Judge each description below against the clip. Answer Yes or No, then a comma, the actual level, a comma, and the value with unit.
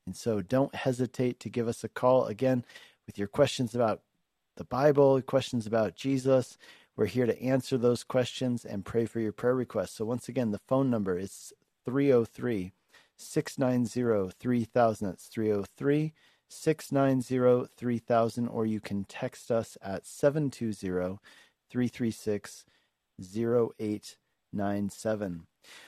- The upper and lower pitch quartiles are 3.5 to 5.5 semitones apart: No, average, 3.1 semitones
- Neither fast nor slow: No, slow, 125 wpm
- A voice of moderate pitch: No, low, 120 Hz